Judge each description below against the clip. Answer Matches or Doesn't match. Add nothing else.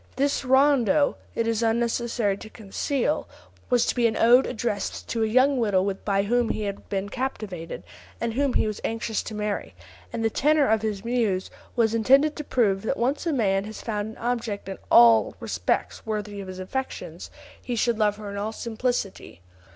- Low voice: Doesn't match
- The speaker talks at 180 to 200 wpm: Matches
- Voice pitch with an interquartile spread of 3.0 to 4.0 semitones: Matches